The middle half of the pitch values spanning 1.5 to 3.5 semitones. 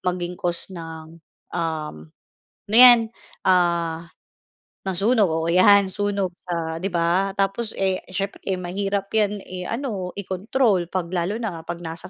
Yes: average, 2.9 semitones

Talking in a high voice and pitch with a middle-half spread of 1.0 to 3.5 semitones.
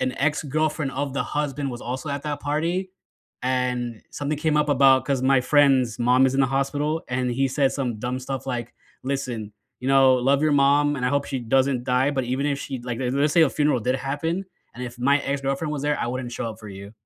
No: low, 135 Hz; narrow, 2.5 semitones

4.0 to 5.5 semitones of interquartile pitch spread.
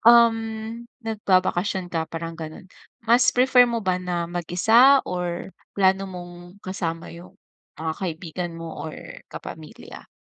Yes: average, 4.5 semitones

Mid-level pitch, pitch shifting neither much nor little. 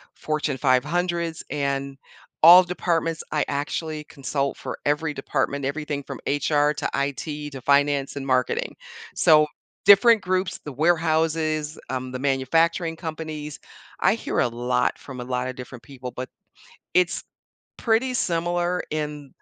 Yes: medium, 150 Hz; average, 3.2 semitones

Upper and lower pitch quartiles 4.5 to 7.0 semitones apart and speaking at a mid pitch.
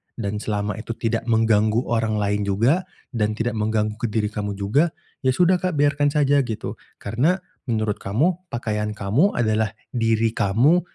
No: average, 4.8 semitones; low, 115 Hz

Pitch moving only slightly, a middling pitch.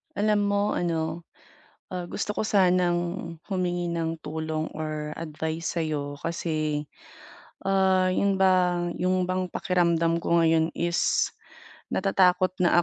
Yes: narrow, 2.3 semitones; medium, 175 Hz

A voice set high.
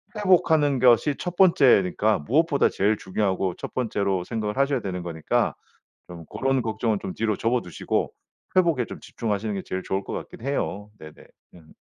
No: low, 110 Hz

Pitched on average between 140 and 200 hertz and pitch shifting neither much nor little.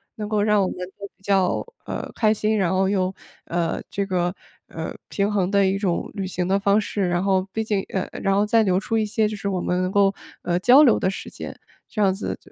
No: high, 195 Hz; narrow, 2.0 semitones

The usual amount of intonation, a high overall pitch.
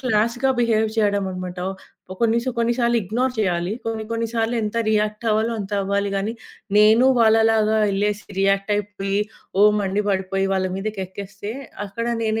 No: narrow, 2.2 semitones; high, 210 Hz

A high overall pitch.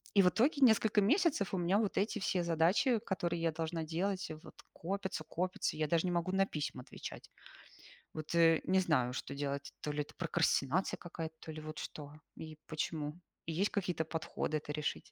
No: medium, 170 Hz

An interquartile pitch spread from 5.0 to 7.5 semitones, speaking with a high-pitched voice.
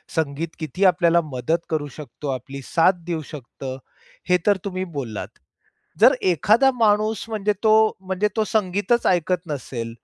No: wide, 5.6 semitones; medium, 175 Hz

